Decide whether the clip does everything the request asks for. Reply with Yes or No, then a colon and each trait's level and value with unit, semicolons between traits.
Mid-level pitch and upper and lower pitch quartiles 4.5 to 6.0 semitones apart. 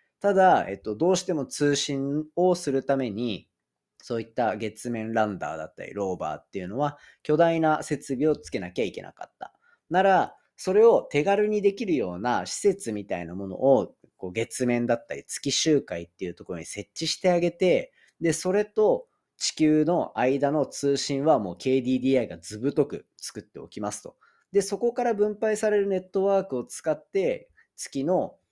No: medium, 150 Hz; wide, 7.9 semitones